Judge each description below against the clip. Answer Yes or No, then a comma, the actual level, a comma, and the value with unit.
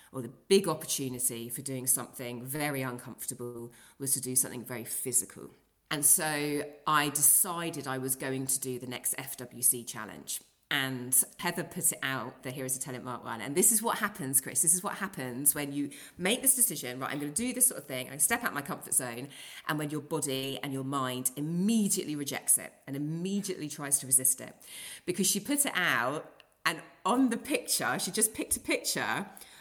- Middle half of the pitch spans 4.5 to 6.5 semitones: Yes, average, 5.1 semitones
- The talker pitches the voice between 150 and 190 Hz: No, medium, 140 Hz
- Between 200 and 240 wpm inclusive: Yes, fast, 205 wpm